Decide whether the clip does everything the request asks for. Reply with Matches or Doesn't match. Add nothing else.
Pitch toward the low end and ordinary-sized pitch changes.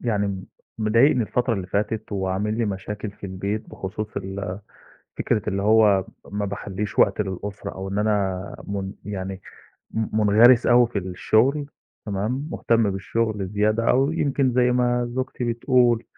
Matches